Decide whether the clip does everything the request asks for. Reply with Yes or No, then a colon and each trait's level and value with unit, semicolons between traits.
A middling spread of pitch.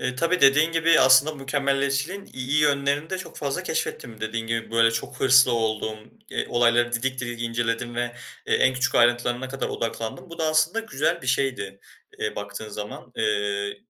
Yes: average, 3.7 semitones